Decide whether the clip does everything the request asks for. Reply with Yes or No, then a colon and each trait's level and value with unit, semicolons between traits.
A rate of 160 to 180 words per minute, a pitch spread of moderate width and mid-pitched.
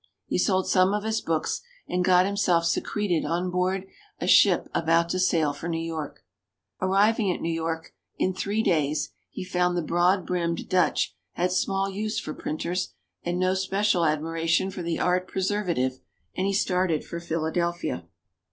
No: average, 165 wpm; narrow, 2.3 semitones; medium, 180 Hz